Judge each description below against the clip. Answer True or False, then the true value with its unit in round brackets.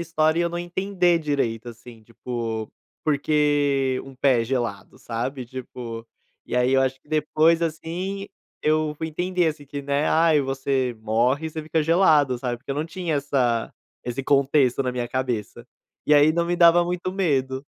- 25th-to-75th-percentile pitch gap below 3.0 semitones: False (4.4 semitones)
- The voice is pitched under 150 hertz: True (140 Hz)